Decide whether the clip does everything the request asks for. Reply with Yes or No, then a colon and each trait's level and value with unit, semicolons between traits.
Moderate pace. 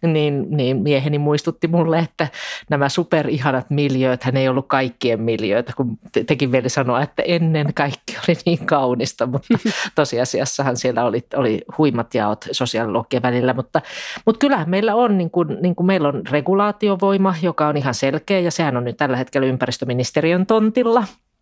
No: fast, 160 wpm